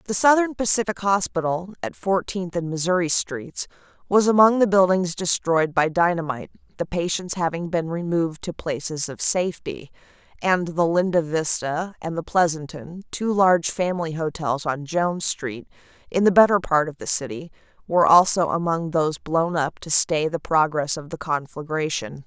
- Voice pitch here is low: No, medium, 170 Hz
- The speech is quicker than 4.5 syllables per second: Yes, 5.0 syllables/s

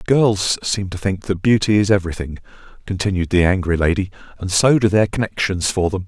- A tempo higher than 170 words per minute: Yes, average, 190 wpm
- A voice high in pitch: No, very low, 95 Hz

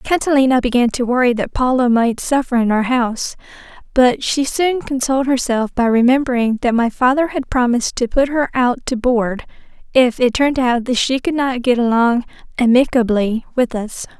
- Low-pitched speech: No, very high, 250 Hz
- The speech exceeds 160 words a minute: Yes, average, 180 wpm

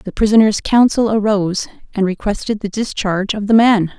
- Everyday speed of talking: Yes, average, 165 wpm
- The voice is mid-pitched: No, high, 210 Hz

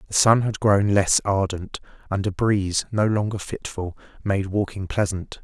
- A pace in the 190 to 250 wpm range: No, average, 165 wpm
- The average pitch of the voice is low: Yes, low, 100 Hz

